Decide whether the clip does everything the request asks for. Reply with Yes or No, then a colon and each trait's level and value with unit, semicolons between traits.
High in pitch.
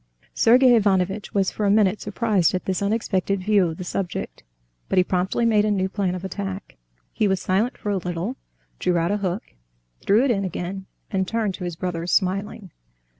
Yes: high, 195 Hz